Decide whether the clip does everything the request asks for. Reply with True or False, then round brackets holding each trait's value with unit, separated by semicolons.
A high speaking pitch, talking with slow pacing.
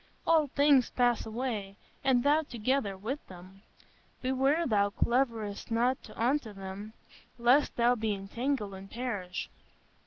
True (235 Hz; 125 wpm)